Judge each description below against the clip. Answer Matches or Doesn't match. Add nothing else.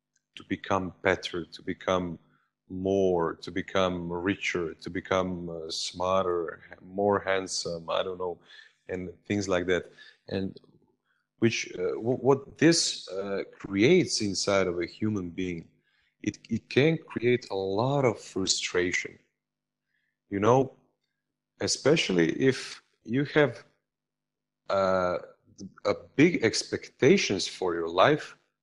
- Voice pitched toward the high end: Doesn't match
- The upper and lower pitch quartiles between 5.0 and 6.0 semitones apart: Doesn't match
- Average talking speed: Doesn't match